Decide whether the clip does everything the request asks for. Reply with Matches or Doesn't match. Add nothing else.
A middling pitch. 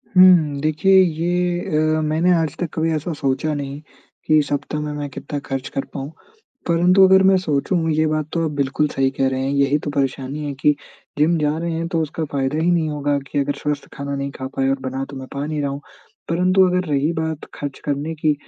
Matches